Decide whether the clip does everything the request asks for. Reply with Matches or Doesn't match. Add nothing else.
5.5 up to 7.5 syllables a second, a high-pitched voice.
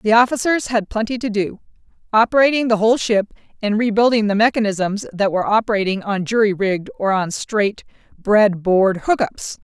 Doesn't match